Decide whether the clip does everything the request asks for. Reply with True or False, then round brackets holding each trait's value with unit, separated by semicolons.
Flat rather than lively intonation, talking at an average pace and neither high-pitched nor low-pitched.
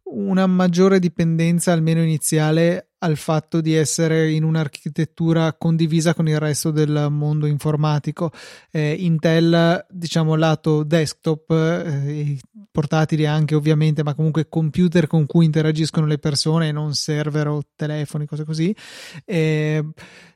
True (1.6 semitones; 125 wpm; 160 Hz)